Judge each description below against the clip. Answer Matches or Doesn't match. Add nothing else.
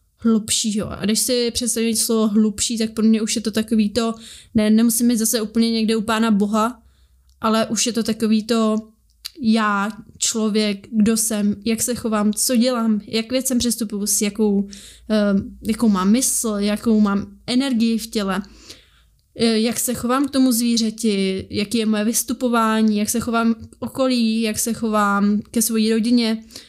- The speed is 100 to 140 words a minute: Doesn't match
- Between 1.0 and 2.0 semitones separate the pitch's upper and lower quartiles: Matches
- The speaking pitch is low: Doesn't match